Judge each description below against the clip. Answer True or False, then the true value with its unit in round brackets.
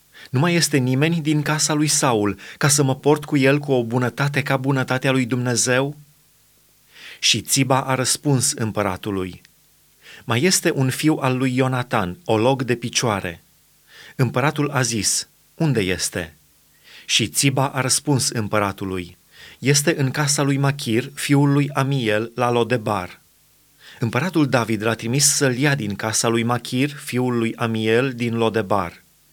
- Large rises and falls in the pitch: False (3.9 semitones)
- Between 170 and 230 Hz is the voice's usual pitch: False (130 Hz)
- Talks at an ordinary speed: True (145 wpm)